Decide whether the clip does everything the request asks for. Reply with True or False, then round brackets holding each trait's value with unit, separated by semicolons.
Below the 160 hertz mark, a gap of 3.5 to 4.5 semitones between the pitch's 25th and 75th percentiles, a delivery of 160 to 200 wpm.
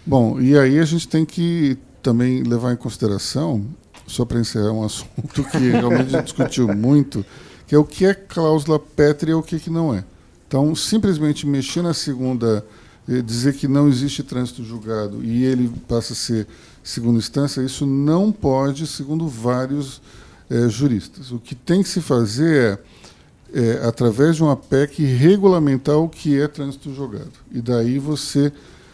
True (135 Hz; 3.9 semitones; 170 wpm)